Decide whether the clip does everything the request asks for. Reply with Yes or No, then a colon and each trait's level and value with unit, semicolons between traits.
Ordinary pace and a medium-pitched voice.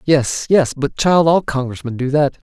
Yes: average, 190 wpm; medium, 145 Hz